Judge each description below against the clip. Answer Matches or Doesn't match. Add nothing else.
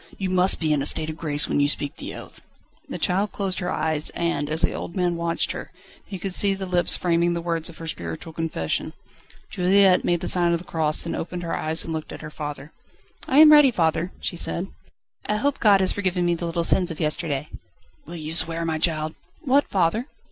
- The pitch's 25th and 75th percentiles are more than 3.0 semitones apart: Doesn't match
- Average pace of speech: Doesn't match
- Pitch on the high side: Doesn't match